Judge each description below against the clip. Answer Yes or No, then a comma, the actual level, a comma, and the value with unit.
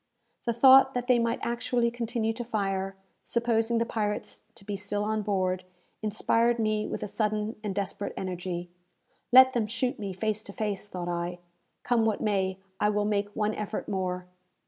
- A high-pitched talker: Yes, high, 210 Hz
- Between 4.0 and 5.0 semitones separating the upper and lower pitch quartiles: No, average, 2.9 semitones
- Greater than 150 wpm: Yes, average, 175 wpm